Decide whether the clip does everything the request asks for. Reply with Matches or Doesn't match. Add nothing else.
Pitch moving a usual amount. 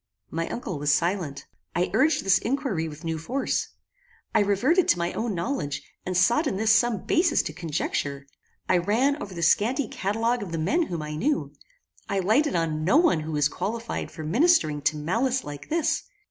Doesn't match